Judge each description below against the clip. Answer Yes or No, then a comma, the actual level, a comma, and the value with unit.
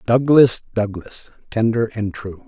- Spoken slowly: Yes, slow, 120 wpm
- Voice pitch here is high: No, low, 110 Hz